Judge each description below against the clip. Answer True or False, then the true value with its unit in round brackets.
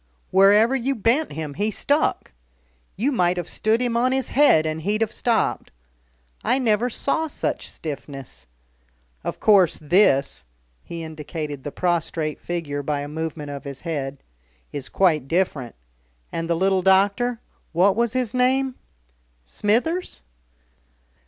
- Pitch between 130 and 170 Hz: False (185 Hz)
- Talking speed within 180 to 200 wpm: False (140 wpm)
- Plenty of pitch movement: True (7.3 semitones)